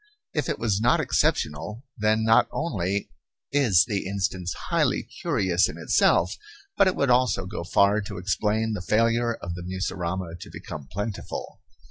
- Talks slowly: No, average, 155 wpm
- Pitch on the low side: Yes, low, 100 Hz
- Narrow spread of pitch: No, average, 3.9 semitones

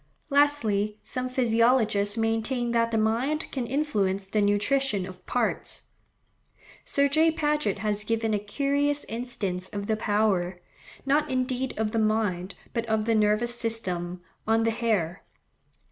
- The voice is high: Yes, high, 225 Hz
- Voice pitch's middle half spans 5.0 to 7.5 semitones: No, average, 3.7 semitones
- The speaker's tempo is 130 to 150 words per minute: Yes, average, 140 wpm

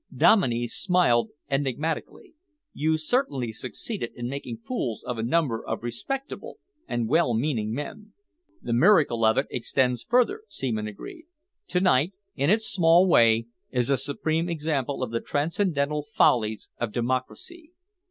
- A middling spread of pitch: No, wide, 6.3 semitones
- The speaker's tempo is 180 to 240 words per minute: No, average, 140 wpm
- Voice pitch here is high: No, medium, 140 Hz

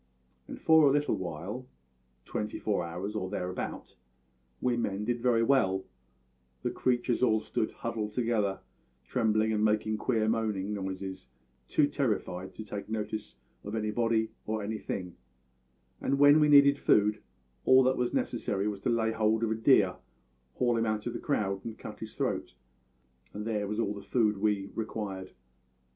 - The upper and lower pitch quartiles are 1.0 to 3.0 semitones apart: Yes, average, 2.7 semitones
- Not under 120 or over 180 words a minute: Yes, average, 160 wpm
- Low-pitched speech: Yes, low, 110 Hz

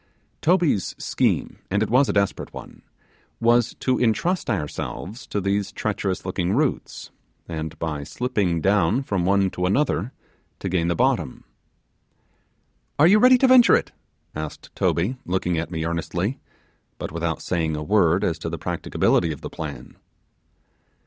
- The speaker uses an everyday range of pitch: No, wide, 6.2 semitones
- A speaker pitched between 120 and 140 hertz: No, very low, 95 Hz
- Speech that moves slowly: No, average, 150 wpm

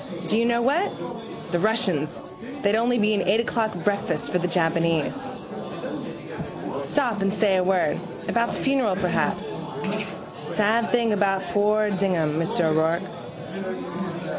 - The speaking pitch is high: Yes, high, 195 Hz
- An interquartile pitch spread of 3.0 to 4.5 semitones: Yes, average, 4.0 semitones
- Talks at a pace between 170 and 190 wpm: No, slow, 135 wpm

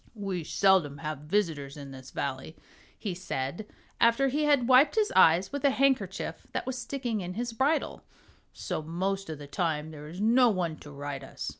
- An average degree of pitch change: No, wide, 8.0 semitones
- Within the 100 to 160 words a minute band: No, average, 185 wpm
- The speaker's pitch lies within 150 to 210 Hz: Yes, medium, 185 Hz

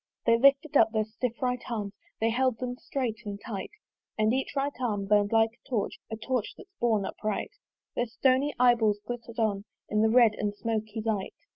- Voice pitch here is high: Yes, high, 225 Hz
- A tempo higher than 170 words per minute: Yes, average, 195 wpm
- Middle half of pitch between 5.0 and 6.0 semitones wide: No, average, 2.7 semitones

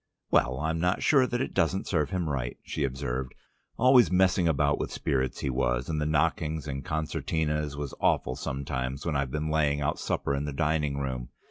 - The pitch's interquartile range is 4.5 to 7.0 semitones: No, average, 2.9 semitones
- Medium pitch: No, very low, 75 Hz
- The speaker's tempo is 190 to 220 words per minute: Yes, average, 195 wpm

